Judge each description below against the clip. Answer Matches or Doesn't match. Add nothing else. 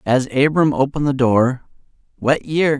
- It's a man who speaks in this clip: Matches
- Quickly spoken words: Doesn't match